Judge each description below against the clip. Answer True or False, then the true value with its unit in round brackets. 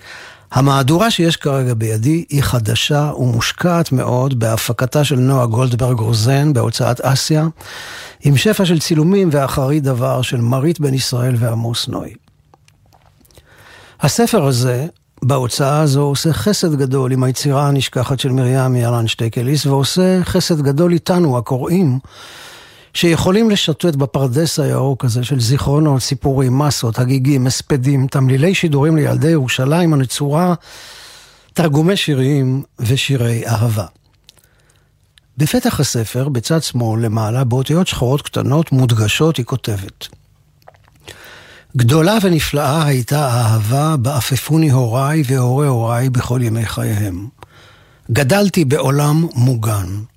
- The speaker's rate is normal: True (110 wpm)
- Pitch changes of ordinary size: True (3.5 semitones)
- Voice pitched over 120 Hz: True (135 Hz)